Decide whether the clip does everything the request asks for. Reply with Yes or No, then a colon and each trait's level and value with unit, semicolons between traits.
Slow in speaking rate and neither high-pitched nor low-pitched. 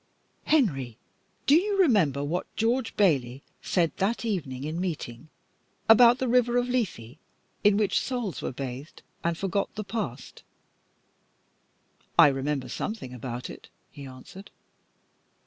Yes: slow, 130 wpm; medium, 180 Hz